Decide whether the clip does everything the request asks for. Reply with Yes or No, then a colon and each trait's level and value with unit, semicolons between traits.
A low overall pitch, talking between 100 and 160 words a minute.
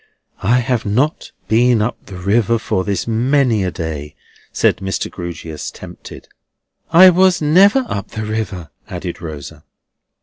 Yes: low, 110 Hz; average, 140 wpm